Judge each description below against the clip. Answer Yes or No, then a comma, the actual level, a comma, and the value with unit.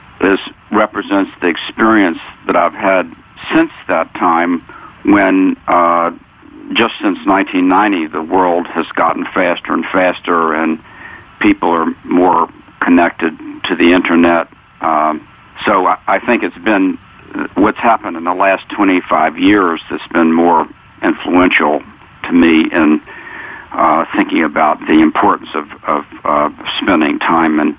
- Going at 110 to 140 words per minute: Yes, slow, 135 wpm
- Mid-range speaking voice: No, low, 110 Hz